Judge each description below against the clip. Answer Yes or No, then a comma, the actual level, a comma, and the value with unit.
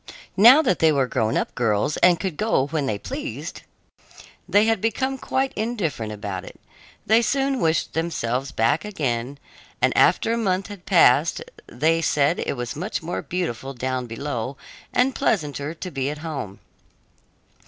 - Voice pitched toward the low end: No, medium, 155 Hz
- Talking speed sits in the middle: Yes, average, 160 wpm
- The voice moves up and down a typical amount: No, wide, 7.5 semitones